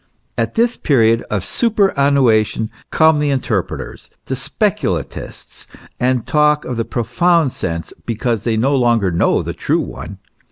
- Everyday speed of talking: Yes, average, 145 wpm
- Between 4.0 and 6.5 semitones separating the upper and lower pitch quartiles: Yes, average, 5.1 semitones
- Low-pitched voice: Yes, low, 125 Hz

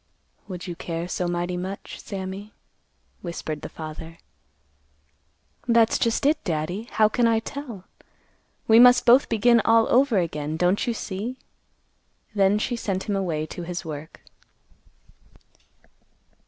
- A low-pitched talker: No, high, 195 Hz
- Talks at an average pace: No, slow, 130 wpm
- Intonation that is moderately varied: Yes, average, 4.8 semitones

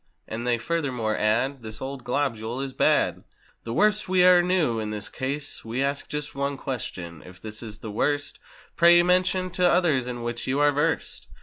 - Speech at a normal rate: Yes, average, 185 wpm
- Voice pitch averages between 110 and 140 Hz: Yes, low, 135 Hz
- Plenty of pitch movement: Yes, wide, 6.1 semitones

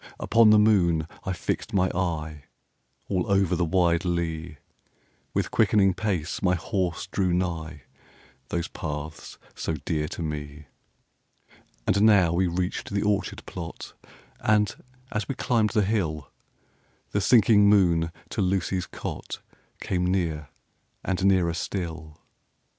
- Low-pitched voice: Yes, very low, 90 Hz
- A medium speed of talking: No, slow, 130 wpm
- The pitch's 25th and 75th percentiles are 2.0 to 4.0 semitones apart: Yes, average, 3.4 semitones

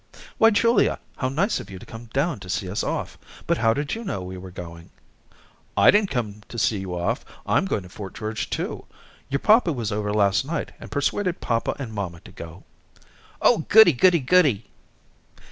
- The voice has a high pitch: No, low, 115 Hz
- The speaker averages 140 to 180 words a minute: No, average, 195 wpm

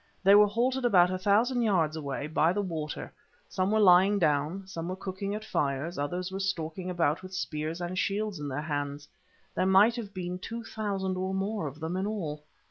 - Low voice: No, medium, 185 Hz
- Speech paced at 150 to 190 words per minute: No, fast, 205 wpm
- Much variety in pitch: No, average, 4.2 semitones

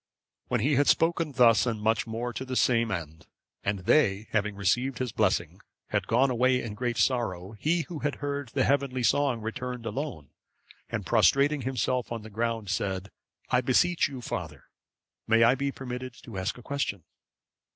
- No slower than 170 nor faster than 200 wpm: Yes, average, 175 wpm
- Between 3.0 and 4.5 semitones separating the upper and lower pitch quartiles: Yes, average, 4.0 semitones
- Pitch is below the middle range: Yes, low, 120 Hz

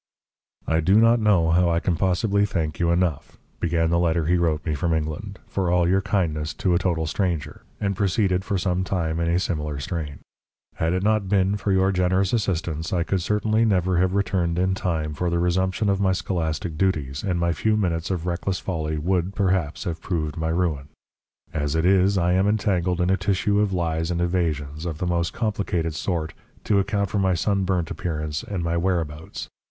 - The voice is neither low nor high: No, very low, 90 Hz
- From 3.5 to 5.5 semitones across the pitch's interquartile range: No, average, 2.9 semitones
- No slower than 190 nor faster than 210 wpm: Yes, average, 200 wpm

